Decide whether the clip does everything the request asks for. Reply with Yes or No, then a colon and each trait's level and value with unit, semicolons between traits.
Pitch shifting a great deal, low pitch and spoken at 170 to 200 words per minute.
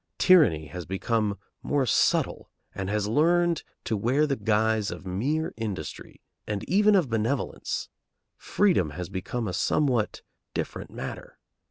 No: wide, 7.1 semitones; low, 110 Hz; slow, 135 wpm